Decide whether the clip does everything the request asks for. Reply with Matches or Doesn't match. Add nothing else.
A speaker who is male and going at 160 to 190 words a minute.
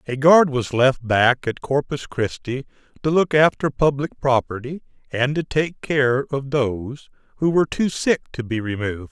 Matches